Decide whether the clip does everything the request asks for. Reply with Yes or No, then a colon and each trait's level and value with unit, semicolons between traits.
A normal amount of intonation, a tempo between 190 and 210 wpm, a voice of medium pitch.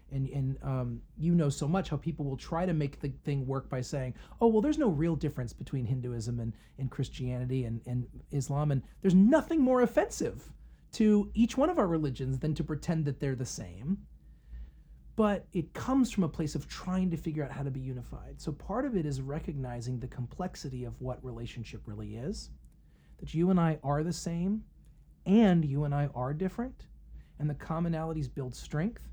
No: wide, 5.8 semitones; average, 200 wpm; medium, 145 Hz